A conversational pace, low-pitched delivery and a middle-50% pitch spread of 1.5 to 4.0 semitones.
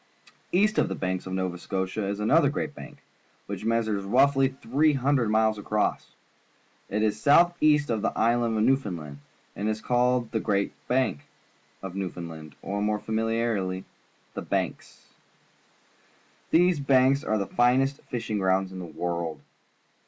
No: average, 150 wpm; low, 110 Hz; average, 5.2 semitones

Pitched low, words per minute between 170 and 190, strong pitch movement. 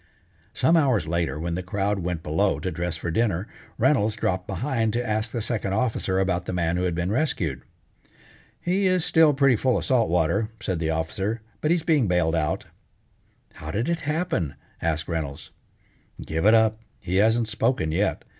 Yes: low, 100 Hz; average, 185 wpm; wide, 5.8 semitones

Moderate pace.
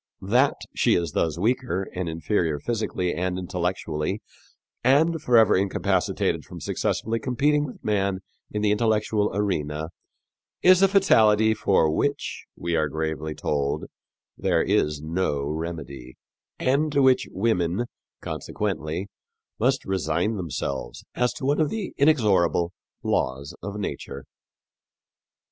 No: slow, 120 wpm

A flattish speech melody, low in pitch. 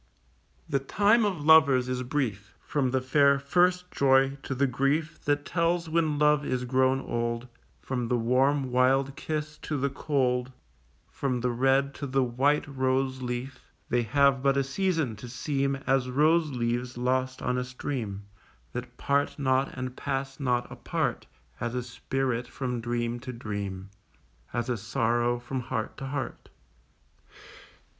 Yes: narrow, 2.3 semitones; low, 130 Hz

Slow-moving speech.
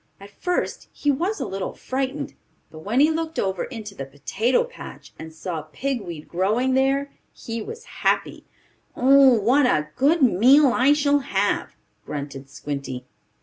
No: average, 155 wpm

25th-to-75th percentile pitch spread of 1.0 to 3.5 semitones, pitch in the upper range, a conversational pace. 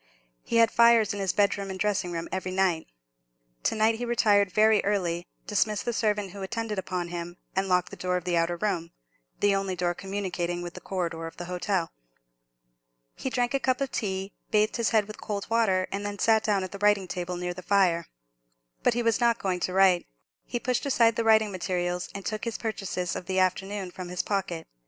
No: average, 3.1 semitones; high, 195 Hz; fast, 210 wpm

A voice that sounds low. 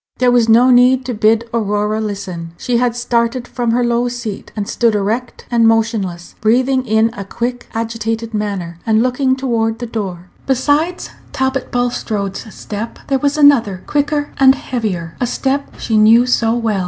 No: high, 230 Hz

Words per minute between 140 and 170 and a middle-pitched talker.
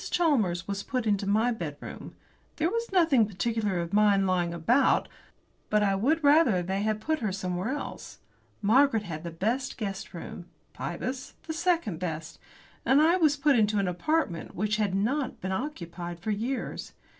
No: average, 165 wpm; high, 210 Hz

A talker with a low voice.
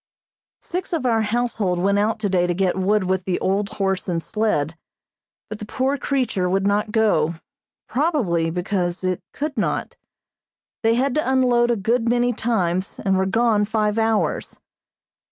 No: high, 210 Hz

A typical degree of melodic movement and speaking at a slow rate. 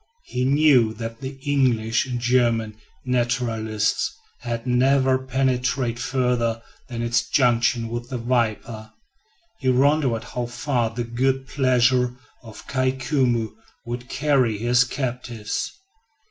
No: narrow, 2.0 semitones; slow, 120 wpm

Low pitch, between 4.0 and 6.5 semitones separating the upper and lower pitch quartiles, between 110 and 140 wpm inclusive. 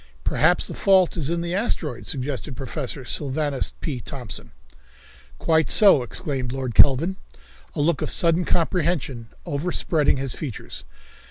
No: medium, 145 Hz; average, 4.3 semitones; slow, 135 wpm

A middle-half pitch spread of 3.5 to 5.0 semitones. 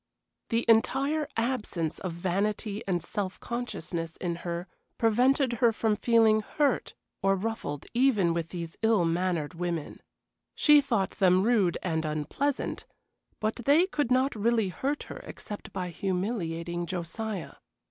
No: wide, 5.5 semitones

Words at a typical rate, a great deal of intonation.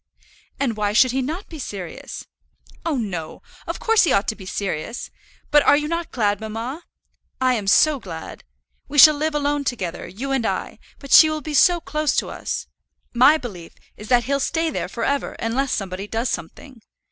Yes: average, 195 wpm; wide, 5.9 semitones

